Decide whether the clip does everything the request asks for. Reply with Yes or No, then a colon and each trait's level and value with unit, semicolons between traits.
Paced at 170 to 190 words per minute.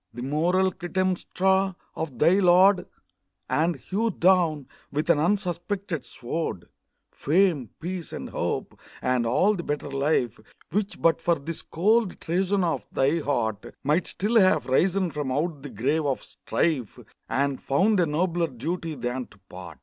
No: average, 150 wpm